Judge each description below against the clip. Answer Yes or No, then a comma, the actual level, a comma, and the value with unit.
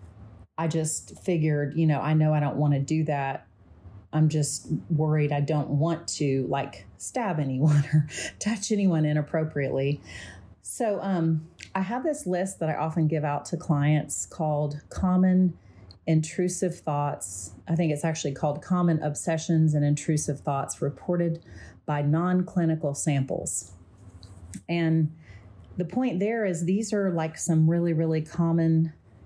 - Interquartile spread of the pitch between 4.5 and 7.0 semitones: No, average, 3.0 semitones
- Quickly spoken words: No, average, 145 wpm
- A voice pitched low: No, medium, 155 Hz